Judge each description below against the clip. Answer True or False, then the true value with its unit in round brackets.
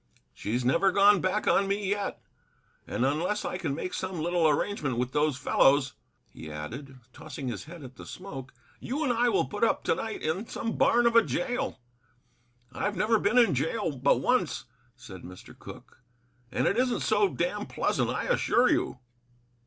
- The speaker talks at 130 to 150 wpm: False (180 wpm)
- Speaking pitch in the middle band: True (180 Hz)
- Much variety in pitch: True (8.3 semitones)